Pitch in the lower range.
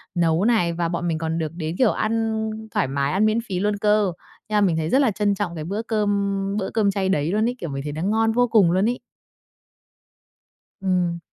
No: high, 195 Hz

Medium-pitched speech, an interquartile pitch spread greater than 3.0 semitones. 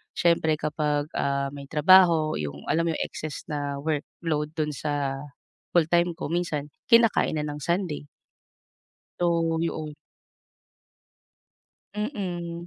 No: medium, 155 Hz; average, 2.7 semitones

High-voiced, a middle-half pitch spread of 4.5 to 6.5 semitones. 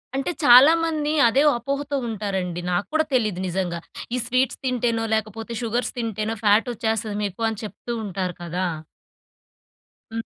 No: high, 225 Hz; average, 3.9 semitones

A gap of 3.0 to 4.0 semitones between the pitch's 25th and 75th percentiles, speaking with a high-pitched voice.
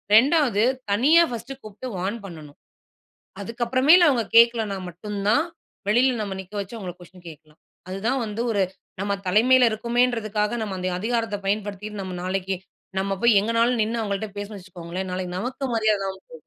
Yes: average, 3.7 semitones; high, 210 Hz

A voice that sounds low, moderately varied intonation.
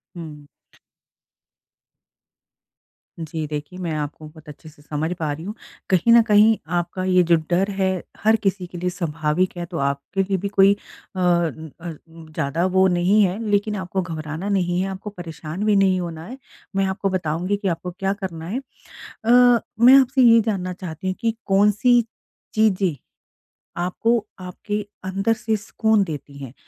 No: medium, 185 Hz; average, 3.6 semitones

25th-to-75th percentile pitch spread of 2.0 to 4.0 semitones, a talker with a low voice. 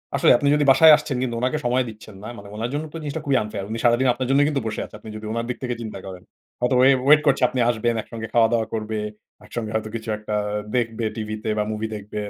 Yes: average, 3.1 semitones; low, 115 Hz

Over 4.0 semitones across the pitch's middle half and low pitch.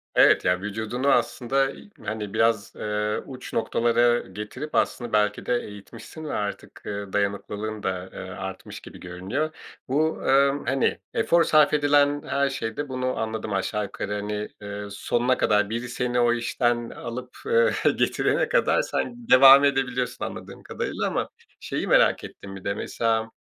Yes: average, 4.6 semitones; low, 120 Hz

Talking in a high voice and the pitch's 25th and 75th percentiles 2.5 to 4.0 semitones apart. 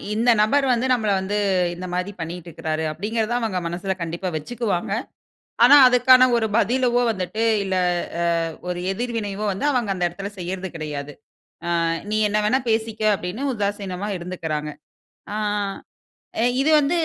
No: high, 200 Hz; average, 4.6 semitones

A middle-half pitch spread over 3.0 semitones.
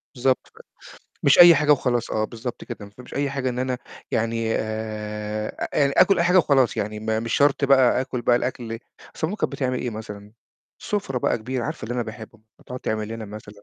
Yes: average, 3.7 semitones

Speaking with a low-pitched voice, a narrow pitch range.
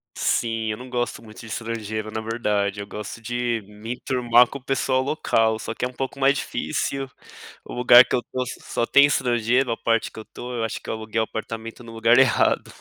Yes: low, 115 Hz; narrow, 2.2 semitones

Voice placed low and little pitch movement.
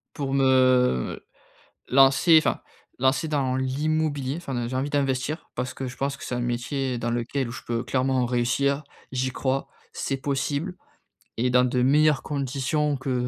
Yes: low, 130 Hz; narrow, 2.0 semitones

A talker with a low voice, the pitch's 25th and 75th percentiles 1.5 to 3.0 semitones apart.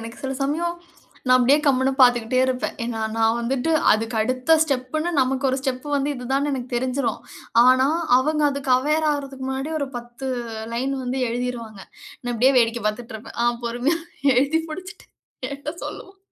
No: very high, 260 Hz; narrow, 2.6 semitones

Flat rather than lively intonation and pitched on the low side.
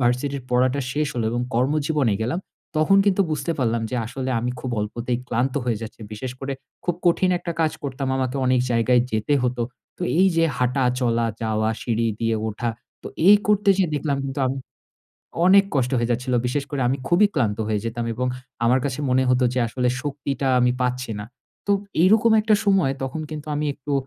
No: average, 3.7 semitones; low, 130 Hz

